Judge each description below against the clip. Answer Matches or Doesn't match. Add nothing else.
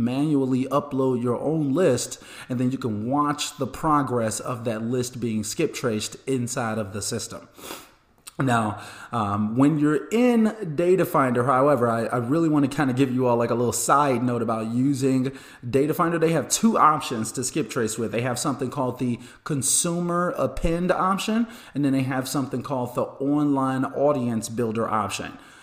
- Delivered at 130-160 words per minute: Doesn't match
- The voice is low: Matches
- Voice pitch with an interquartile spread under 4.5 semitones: Matches